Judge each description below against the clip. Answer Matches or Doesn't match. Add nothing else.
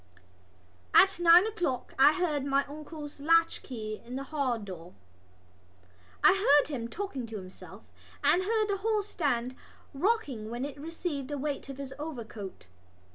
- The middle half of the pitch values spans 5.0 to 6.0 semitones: Matches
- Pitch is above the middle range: Matches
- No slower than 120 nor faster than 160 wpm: Matches